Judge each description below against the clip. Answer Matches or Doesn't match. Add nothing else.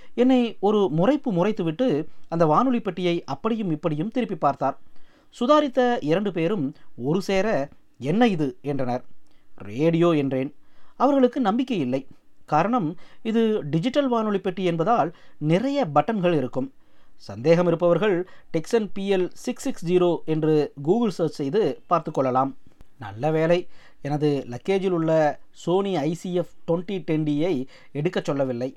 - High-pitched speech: Doesn't match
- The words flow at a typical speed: Matches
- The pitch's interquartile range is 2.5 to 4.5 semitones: Doesn't match